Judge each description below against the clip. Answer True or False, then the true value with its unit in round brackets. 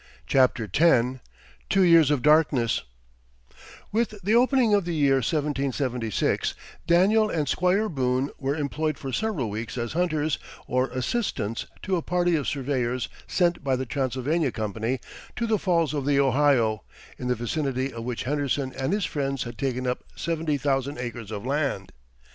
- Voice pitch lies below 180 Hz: True (140 Hz)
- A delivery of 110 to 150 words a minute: False (160 wpm)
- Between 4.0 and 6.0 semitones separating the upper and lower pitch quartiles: True (4.7 semitones)